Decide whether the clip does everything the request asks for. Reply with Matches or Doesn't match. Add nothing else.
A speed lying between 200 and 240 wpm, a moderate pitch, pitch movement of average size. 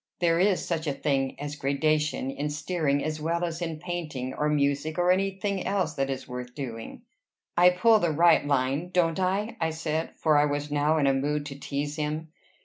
Matches